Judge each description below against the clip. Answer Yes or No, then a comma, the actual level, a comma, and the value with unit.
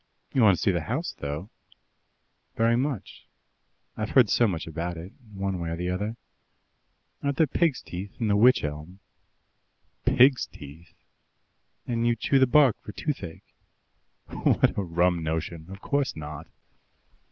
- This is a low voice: Yes, low, 100 Hz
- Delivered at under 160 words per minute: Yes, average, 150 wpm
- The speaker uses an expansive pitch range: Yes, wide, 6.7 semitones